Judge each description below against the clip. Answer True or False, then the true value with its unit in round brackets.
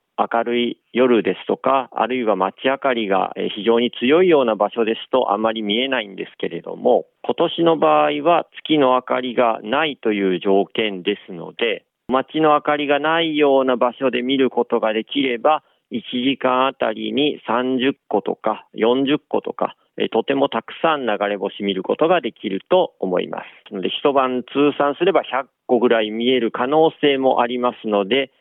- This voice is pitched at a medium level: False (125 Hz)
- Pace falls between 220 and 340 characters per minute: True (315 characters per minute)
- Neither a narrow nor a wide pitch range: True (4.0 semitones)